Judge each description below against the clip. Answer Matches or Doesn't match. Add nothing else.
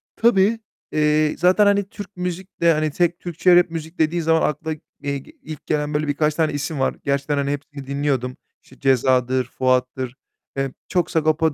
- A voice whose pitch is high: Doesn't match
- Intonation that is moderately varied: Matches